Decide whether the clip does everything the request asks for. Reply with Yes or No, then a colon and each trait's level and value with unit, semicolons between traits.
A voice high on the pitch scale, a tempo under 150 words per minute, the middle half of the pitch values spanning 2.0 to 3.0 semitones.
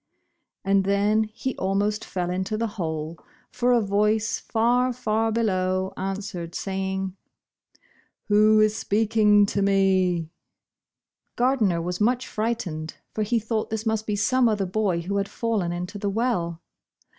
Yes: high, 205 Hz; average, 140 wpm; average, 2.7 semitones